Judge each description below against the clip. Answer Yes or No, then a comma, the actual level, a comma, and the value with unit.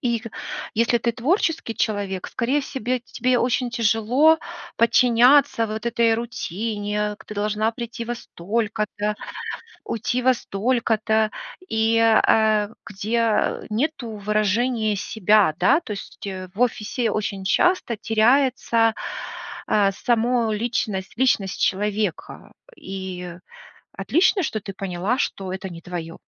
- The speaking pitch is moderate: No, high, 220 Hz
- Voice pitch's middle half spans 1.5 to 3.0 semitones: Yes, average, 2.7 semitones